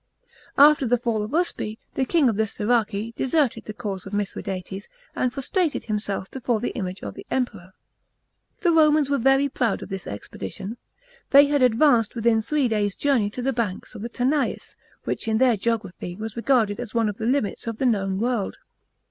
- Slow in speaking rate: No, average, 190 wpm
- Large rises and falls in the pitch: No, average, 4.2 semitones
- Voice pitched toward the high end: Yes, high, 230 Hz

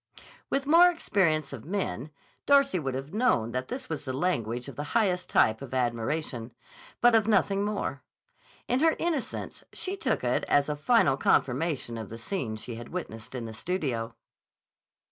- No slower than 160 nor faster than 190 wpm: Yes, average, 170 wpm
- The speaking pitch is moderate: Yes, medium, 150 Hz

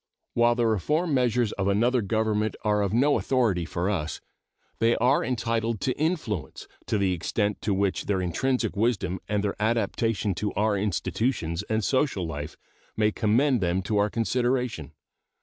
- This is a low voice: Yes, low, 110 Hz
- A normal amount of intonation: Yes, average, 3.5 semitones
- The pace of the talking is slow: No, average, 160 wpm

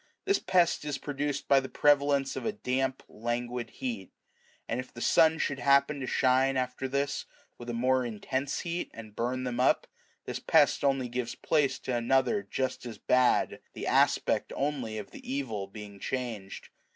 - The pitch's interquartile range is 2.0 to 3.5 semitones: Yes, narrow, 2.6 semitones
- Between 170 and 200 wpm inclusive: Yes, average, 175 wpm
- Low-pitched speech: Yes, low, 130 Hz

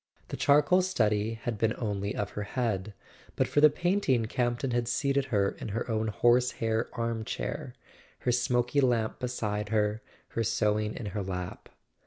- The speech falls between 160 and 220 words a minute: Yes, average, 165 wpm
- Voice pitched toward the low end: Yes, low, 115 Hz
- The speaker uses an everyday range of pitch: Yes, average, 3.0 semitones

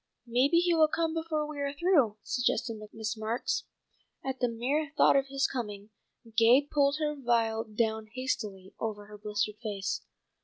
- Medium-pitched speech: No, high, 245 Hz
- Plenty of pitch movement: No, average, 4.7 semitones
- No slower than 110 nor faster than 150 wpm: No, average, 160 wpm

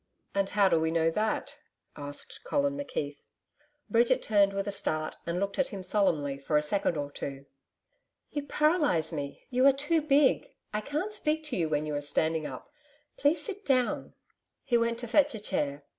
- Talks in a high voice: Yes, high, 200 Hz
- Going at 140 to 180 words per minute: No, average, 190 wpm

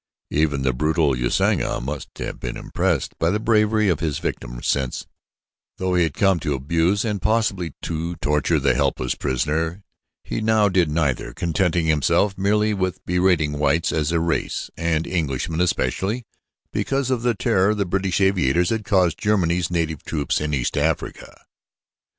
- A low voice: Yes, very low, 85 Hz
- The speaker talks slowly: No, average, 160 wpm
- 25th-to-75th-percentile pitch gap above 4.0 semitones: Yes, average, 4.7 semitones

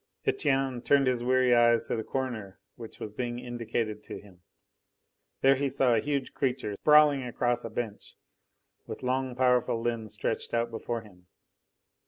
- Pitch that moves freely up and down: No, narrow, 2.5 semitones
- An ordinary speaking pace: Yes, average, 160 wpm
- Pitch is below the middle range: Yes, low, 120 Hz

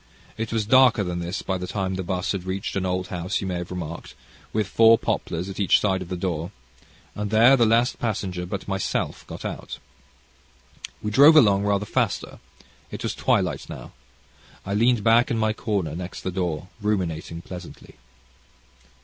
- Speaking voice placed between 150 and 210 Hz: No, very low, 95 Hz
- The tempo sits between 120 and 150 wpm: No, average, 180 wpm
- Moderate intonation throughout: Yes, average, 3.2 semitones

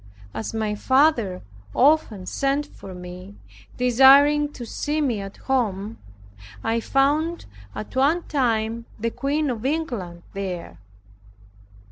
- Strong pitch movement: Yes, wide, 5.9 semitones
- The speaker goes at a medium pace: No, slow, 115 wpm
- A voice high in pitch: Yes, high, 245 Hz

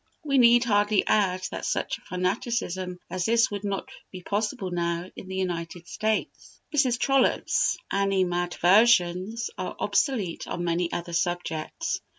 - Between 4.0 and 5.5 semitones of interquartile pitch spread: Yes, average, 4.5 semitones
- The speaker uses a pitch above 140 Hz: Yes, high, 190 Hz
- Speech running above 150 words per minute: No, slow, 135 wpm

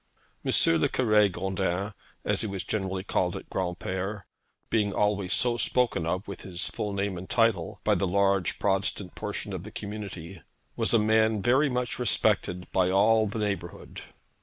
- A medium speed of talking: Yes, average, 165 wpm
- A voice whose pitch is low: Yes, low, 100 Hz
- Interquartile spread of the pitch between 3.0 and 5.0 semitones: No, narrow, 2.4 semitones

